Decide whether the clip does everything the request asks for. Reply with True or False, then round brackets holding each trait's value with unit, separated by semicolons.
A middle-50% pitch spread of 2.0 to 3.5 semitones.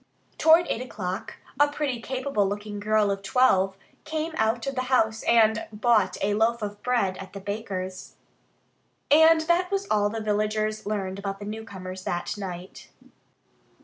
False (4.1 semitones)